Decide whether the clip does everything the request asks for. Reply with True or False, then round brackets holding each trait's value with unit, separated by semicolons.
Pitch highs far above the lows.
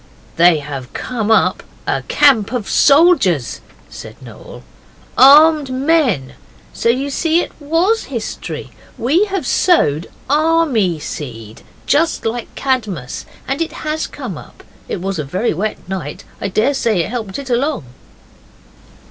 True (8.9 semitones)